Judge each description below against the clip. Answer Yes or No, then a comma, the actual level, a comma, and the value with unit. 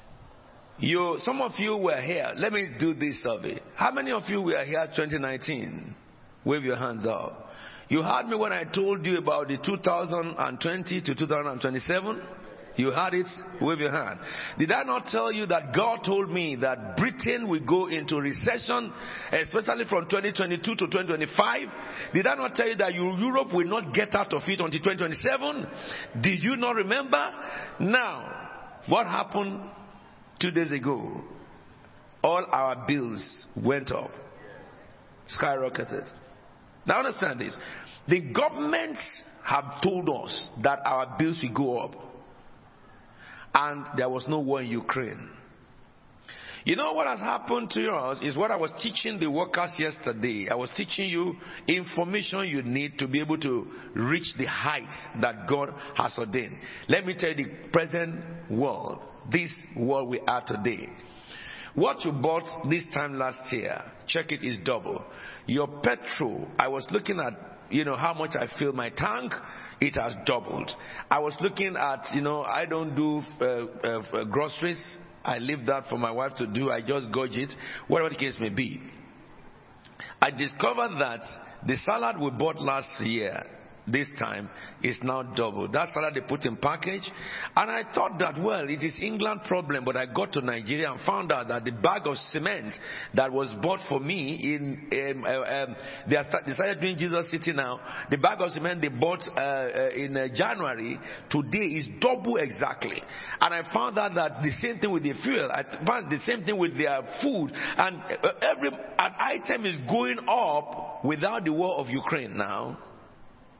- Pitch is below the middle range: No, medium, 155 Hz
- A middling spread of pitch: Yes, average, 5.0 semitones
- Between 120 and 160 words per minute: No, average, 170 wpm